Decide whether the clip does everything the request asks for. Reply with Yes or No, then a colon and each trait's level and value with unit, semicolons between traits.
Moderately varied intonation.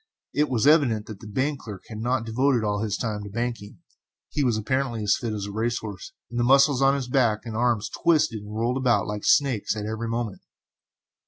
Yes: average, 3.5 semitones